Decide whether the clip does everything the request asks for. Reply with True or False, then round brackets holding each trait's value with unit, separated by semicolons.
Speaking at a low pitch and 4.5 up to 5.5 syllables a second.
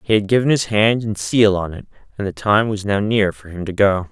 True (105 Hz; 5.4 syllables/s)